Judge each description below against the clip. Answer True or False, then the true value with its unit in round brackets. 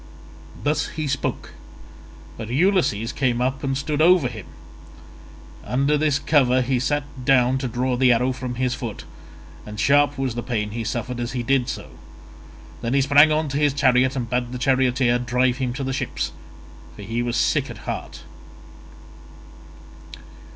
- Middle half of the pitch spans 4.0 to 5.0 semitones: False (2.4 semitones)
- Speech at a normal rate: True (165 wpm)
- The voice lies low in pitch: True (130 Hz)